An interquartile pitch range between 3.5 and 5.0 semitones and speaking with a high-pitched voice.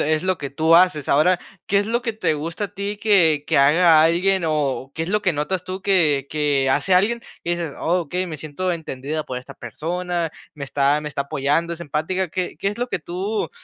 No: average, 3.9 semitones; medium, 165 Hz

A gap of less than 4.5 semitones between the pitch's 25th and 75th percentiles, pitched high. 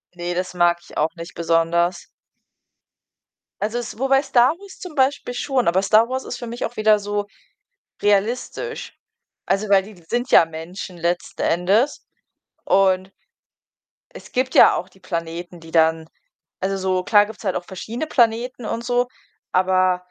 No: wide, 5.4 semitones; high, 195 Hz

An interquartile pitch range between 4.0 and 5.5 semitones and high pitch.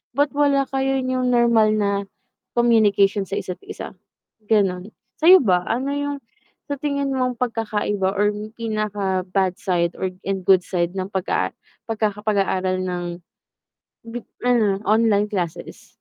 Yes: average, 4.6 semitones; high, 210 Hz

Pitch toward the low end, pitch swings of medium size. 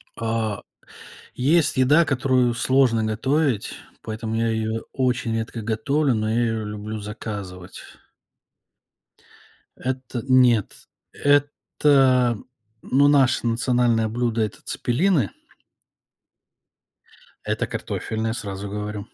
Yes: low, 115 Hz; average, 3.1 semitones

